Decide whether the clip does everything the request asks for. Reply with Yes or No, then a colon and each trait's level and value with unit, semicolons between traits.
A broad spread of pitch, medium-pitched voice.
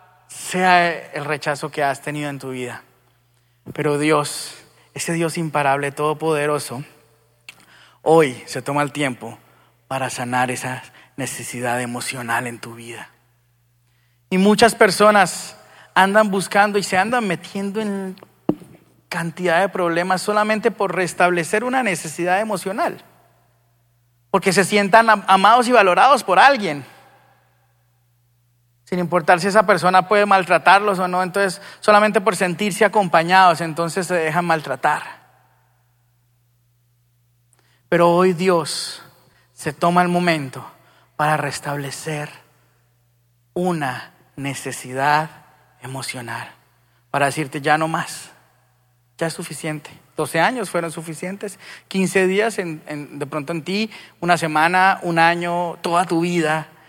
Yes: wide, 6.7 semitones; medium, 155 Hz